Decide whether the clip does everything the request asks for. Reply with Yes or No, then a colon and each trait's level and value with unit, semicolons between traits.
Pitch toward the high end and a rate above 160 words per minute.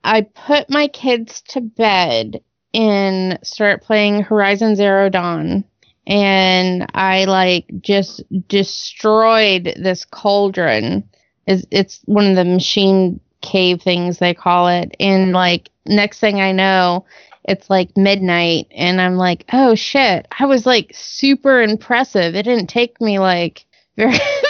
No: high, 195 Hz; slow, 135 wpm